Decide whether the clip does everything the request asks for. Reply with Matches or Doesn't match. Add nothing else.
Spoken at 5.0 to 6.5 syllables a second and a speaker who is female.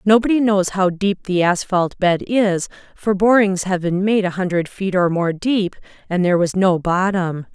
Doesn't match